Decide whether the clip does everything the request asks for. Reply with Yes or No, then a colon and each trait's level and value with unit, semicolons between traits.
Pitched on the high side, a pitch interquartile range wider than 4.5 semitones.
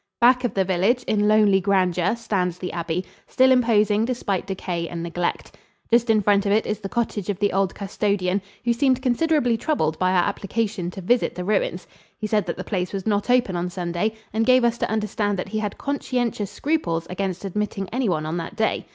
No: high, 205 Hz; average, 4.0 semitones